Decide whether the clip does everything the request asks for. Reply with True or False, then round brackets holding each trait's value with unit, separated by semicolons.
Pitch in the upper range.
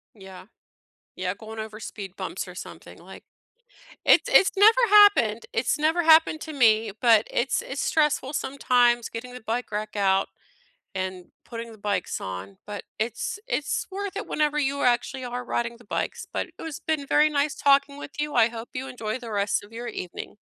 True (240 Hz)